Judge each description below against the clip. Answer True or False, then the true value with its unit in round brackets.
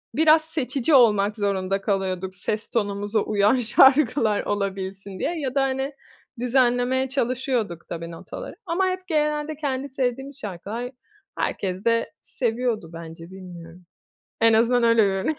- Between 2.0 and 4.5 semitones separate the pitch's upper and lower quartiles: False (5.4 semitones)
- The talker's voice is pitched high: True (230 Hz)